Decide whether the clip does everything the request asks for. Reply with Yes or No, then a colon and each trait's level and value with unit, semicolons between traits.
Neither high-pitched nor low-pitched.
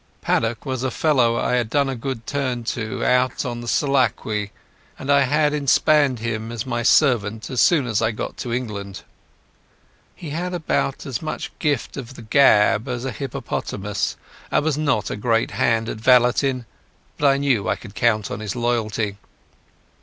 No: low, 120 Hz